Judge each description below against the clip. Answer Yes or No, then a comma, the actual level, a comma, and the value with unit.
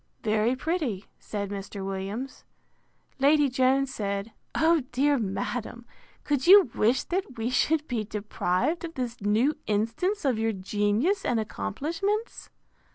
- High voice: Yes, high, 245 Hz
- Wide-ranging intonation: Yes, wide, 6.1 semitones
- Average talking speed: No, slow, 130 wpm